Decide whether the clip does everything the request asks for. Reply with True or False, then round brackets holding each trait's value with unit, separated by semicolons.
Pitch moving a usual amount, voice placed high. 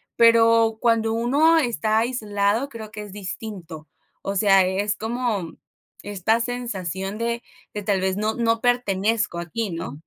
True (3.1 semitones; 215 Hz)